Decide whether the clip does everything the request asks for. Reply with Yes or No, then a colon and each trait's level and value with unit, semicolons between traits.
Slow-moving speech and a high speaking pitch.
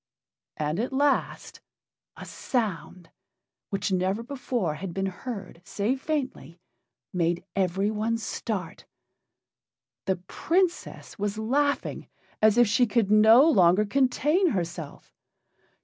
Yes: slow, 105 wpm; high, 210 Hz